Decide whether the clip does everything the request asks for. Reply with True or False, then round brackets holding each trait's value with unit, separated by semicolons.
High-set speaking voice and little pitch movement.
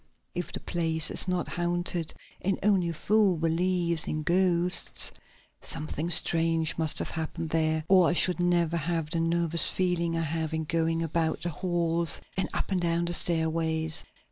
False (170 Hz; 1.4 semitones)